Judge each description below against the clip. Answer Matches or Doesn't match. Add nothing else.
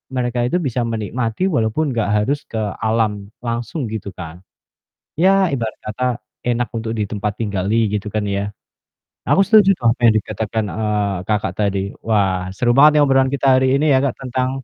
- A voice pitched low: Matches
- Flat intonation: Doesn't match